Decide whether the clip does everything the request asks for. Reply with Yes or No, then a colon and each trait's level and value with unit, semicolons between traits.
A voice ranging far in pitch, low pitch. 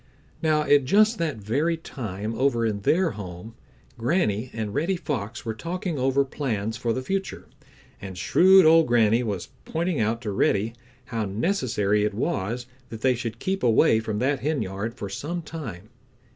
Yes: wide, 6.7 semitones; low, 120 Hz